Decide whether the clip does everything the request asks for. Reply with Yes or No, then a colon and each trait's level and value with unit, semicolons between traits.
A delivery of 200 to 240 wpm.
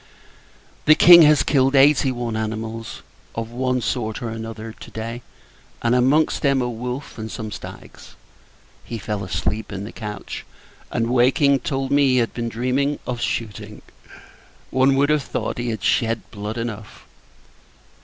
No: average, 155 wpm